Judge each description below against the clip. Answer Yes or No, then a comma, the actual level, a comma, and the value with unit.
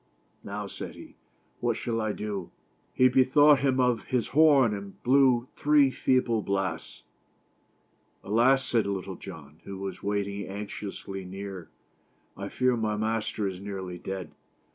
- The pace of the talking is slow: No, average, 150 wpm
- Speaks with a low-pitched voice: Yes, low, 105 Hz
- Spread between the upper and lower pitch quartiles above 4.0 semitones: Yes, average, 4.6 semitones